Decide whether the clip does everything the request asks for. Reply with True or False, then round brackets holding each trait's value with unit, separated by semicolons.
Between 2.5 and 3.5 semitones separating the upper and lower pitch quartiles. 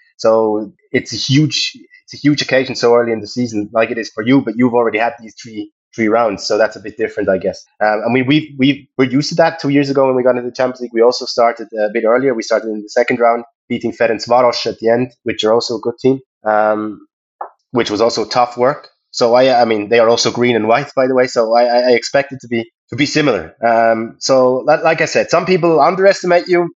True (3.1 semitones)